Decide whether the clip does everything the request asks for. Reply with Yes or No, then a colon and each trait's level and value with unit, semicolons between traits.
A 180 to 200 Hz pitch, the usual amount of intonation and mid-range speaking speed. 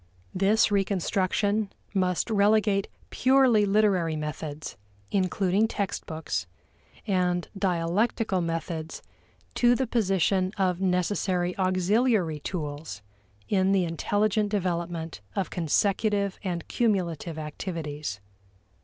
No: medium, 185 Hz; average, 3.5 semitones; slow, 90 wpm